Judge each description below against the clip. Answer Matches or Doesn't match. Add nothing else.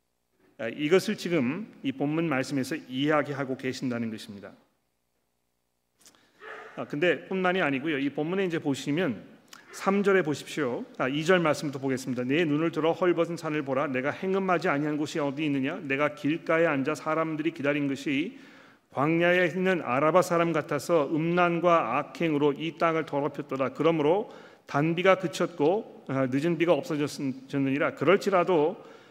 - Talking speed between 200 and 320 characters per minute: Doesn't match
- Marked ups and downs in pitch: Doesn't match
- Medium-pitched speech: Matches